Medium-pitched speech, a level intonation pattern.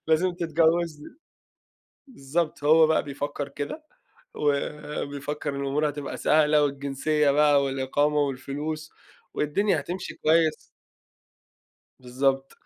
Yes: medium, 150 Hz; narrow, 2.0 semitones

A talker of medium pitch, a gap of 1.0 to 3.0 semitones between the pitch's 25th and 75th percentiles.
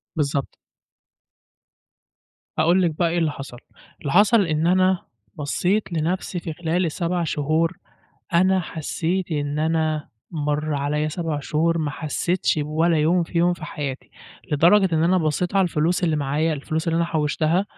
Yes: medium, 160 Hz; narrow, 2.6 semitones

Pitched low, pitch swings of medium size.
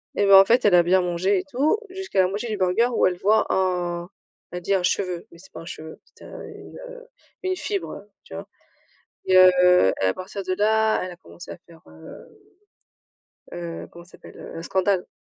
No: medium, 185 Hz; average, 3.1 semitones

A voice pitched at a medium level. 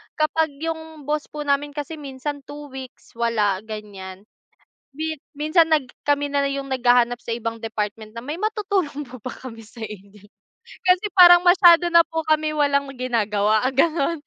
No: very high, 280 Hz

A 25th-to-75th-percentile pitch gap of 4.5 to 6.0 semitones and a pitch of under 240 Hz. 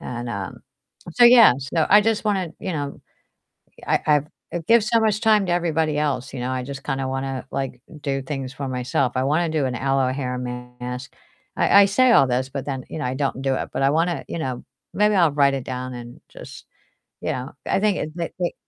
Yes: average, 5.1 semitones; medium, 140 Hz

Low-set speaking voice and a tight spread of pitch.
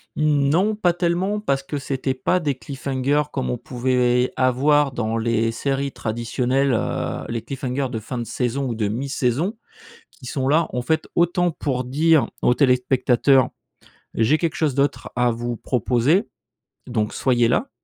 No: low, 130 Hz; average, 3.2 semitones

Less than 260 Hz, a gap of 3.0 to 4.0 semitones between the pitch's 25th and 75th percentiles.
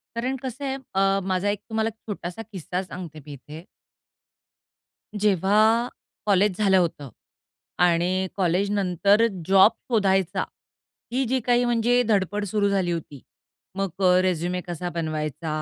Yes: high, 190 Hz; average, 3.3 semitones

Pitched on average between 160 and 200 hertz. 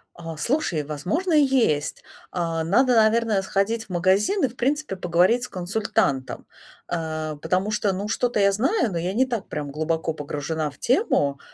Yes: high, 190 Hz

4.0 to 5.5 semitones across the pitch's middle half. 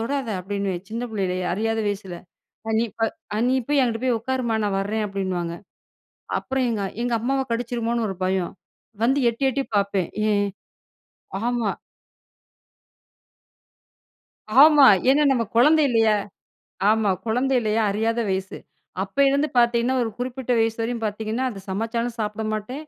No: average, 3.4 semitones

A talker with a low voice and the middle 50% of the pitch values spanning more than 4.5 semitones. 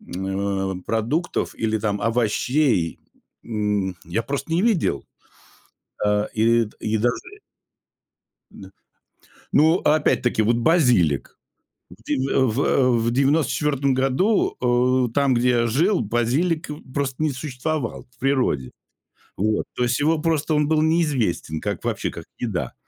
Yes: low, 125 Hz; wide, 5.4 semitones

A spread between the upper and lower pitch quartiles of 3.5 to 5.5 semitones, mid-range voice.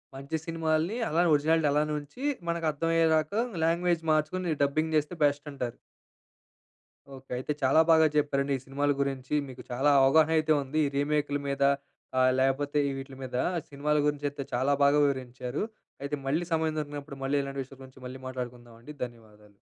No: average, 2.7 semitones; medium, 145 Hz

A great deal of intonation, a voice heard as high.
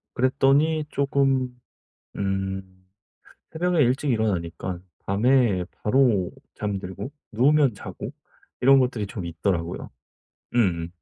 No: wide, 6.1 semitones; low, 110 Hz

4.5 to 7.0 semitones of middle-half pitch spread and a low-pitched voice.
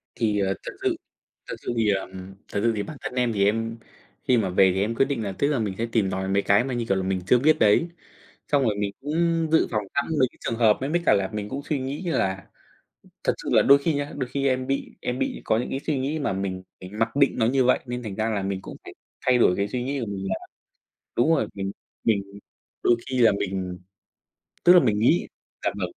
Yes: average, 5.2 semitones; low, 115 Hz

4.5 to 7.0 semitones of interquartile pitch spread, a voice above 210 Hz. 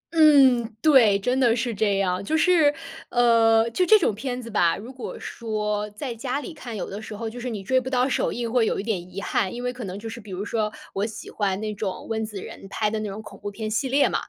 No: average, 3.3 semitones; high, 225 Hz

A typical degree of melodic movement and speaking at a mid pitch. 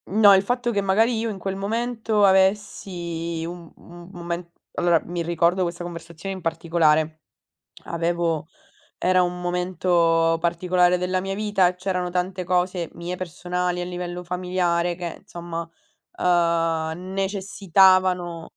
No: narrow, 1.9 semitones; medium, 180 Hz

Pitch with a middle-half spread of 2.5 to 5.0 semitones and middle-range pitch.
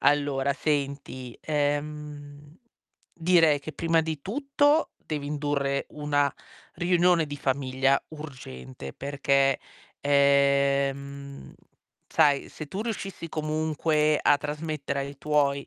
No: narrow, 1.9 semitones; medium, 145 Hz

